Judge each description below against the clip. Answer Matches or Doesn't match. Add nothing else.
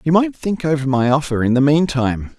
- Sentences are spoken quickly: Matches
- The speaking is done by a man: Matches